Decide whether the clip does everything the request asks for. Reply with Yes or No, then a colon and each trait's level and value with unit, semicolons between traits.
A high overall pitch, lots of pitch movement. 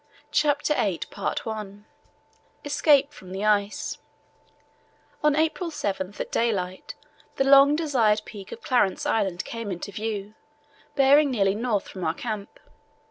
Yes: high, 215 Hz; wide, 5.8 semitones